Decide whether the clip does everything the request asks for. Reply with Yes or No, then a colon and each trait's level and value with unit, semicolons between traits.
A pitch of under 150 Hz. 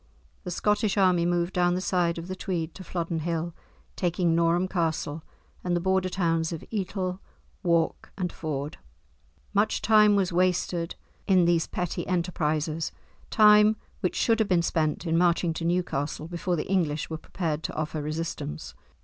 No: medium, 175 Hz